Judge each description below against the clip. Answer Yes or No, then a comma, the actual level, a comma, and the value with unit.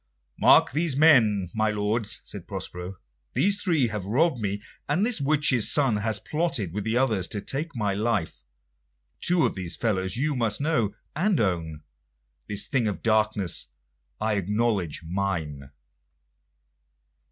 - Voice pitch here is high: No, low, 110 Hz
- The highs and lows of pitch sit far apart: Yes, wide, 5.7 semitones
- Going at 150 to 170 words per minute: No, average, 140 wpm